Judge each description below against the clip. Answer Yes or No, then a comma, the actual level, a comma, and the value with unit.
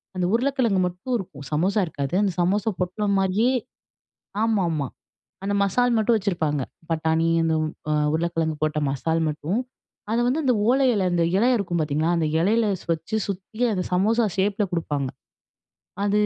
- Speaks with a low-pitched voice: No, medium, 185 Hz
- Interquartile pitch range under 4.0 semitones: No, average, 5.1 semitones